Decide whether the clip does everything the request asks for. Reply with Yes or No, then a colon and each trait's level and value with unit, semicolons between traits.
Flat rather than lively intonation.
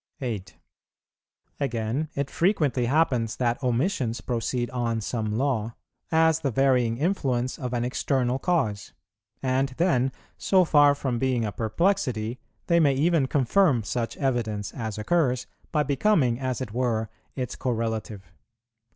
No: average, 3.7 semitones